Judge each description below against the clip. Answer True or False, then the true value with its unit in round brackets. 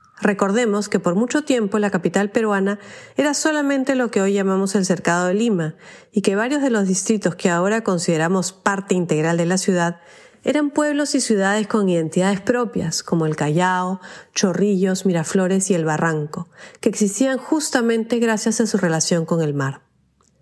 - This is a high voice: True (200 Hz)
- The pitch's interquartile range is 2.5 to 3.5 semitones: False (4.3 semitones)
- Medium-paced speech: True (170 wpm)